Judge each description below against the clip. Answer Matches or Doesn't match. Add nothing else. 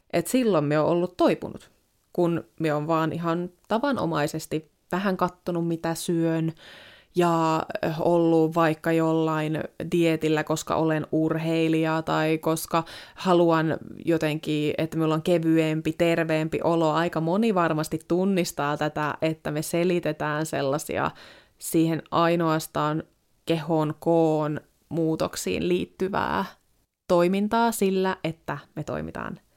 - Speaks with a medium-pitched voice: Matches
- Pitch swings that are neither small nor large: Doesn't match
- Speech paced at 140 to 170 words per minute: Doesn't match